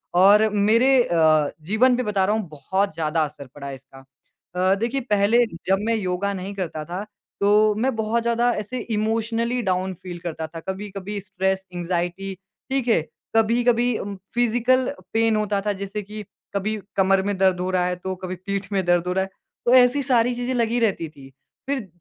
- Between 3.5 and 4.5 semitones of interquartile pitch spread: Yes, average, 3.8 semitones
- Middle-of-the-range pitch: No, high, 200 Hz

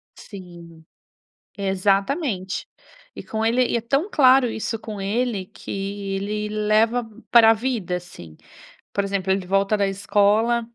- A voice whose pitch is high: Yes, high, 205 Hz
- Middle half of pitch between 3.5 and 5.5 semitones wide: No, average, 2.9 semitones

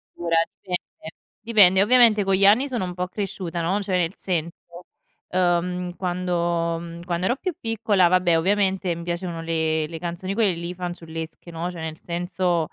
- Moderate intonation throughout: No, narrow, 2.1 semitones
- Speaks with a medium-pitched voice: Yes, medium, 180 Hz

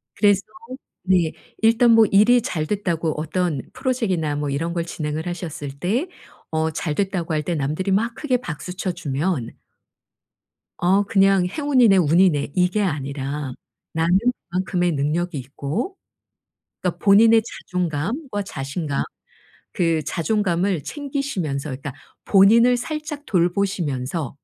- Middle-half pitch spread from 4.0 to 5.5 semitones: Yes, average, 5.1 semitones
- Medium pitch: Yes, medium, 180 Hz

